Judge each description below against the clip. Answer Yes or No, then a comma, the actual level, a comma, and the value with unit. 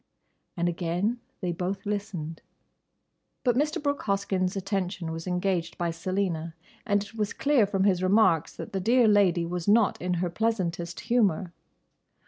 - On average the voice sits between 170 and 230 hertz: Yes, high, 190 Hz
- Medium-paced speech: Yes, average, 150 wpm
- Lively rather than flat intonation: No, average, 3.2 semitones